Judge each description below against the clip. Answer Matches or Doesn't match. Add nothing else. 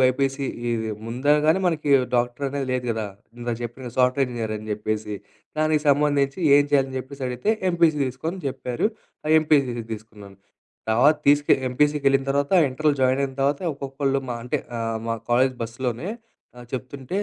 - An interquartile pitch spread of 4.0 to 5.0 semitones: Doesn't match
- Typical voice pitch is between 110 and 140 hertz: Matches